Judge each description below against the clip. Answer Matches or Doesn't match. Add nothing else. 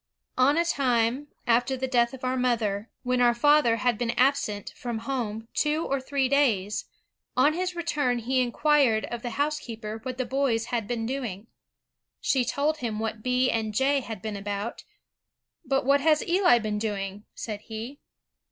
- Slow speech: Doesn't match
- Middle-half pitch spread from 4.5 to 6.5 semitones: Doesn't match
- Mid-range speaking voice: Doesn't match